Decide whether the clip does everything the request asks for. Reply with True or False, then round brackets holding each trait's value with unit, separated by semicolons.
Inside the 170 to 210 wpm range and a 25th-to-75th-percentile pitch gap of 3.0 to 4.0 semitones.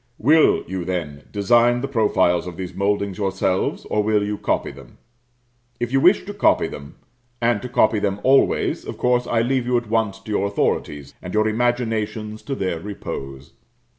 False (180 wpm; 4.4 semitones)